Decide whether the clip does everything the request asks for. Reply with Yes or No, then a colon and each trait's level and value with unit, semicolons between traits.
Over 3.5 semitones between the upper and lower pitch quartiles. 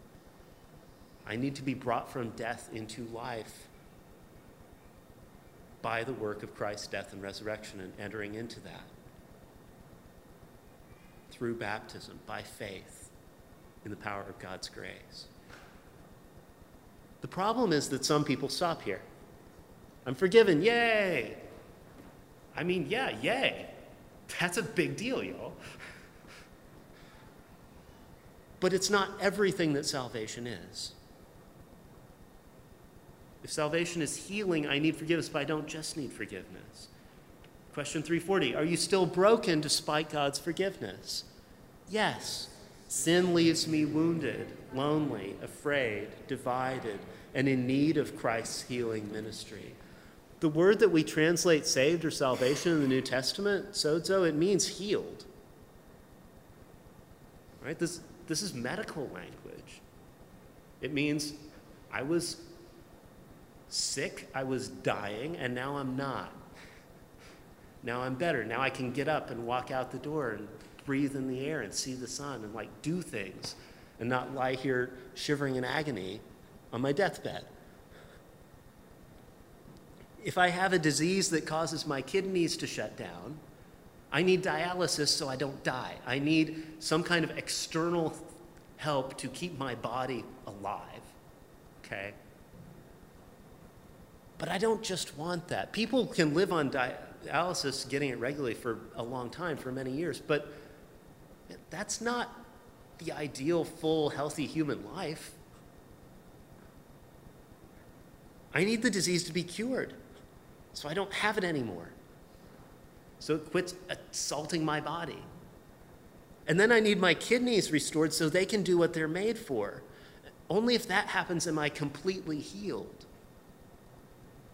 Yes: average, 5.0 semitones